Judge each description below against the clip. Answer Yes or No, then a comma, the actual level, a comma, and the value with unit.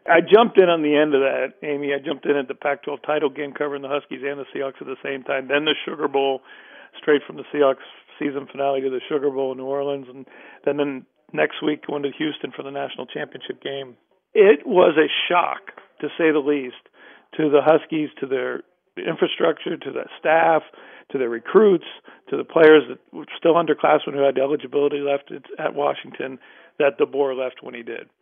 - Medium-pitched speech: Yes, medium, 145 Hz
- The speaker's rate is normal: No, fast, 210 wpm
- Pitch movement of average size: No, narrow, 1.8 semitones